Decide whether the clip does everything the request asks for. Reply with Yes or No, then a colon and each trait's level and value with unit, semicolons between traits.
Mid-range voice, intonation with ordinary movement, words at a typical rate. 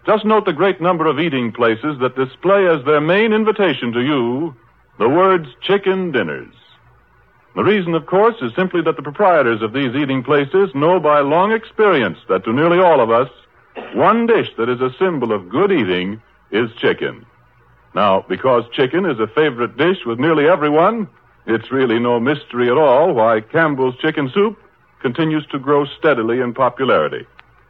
No: medium, 150 Hz; wide, 6.9 semitones; average, 175 wpm